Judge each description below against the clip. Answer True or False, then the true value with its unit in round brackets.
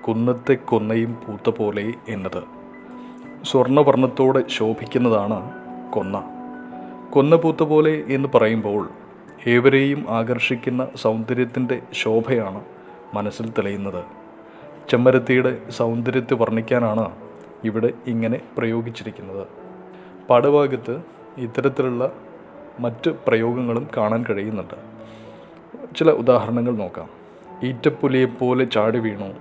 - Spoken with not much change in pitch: False (3.0 semitones)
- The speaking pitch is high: False (120 Hz)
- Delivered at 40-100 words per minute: True (75 wpm)